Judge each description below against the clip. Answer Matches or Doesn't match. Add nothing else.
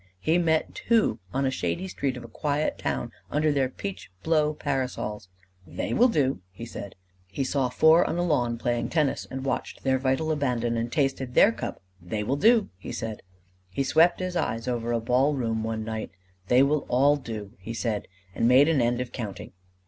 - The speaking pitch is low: Matches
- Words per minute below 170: Doesn't match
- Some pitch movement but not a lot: Matches